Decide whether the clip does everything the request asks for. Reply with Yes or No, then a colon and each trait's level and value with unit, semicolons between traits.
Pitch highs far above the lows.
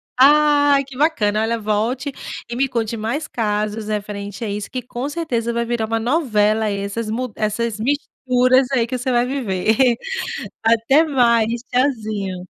No: average, 3.3 semitones